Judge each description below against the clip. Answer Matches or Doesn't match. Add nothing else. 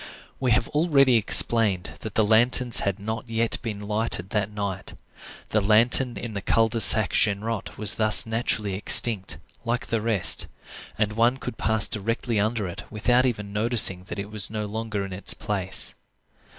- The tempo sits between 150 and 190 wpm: Matches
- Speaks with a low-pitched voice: Matches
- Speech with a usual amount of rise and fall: Doesn't match